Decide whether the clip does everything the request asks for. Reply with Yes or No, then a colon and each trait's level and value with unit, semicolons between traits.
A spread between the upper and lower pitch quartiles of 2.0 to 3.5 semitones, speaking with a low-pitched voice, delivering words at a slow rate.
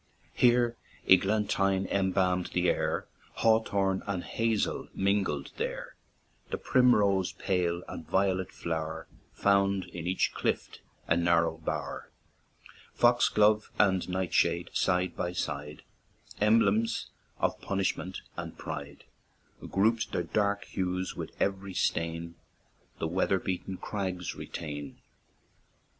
Yes: narrow, 2.6 semitones; very low, 95 Hz; slow, 105 wpm